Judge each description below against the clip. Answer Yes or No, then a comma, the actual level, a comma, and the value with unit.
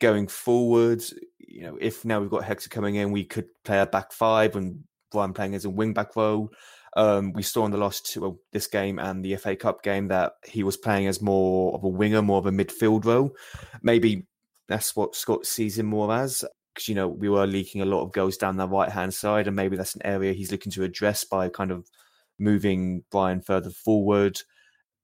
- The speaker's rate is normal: No, fast, 220 wpm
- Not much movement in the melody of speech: Yes, narrow, 2.0 semitones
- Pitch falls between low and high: No, low, 100 Hz